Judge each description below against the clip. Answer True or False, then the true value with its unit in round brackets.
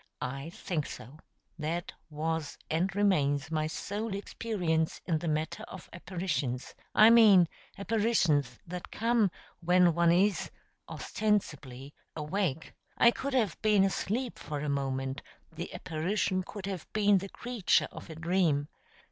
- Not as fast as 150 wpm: True (135 wpm)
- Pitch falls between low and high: True (175 Hz)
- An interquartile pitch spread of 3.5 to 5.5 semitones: True (4.8 semitones)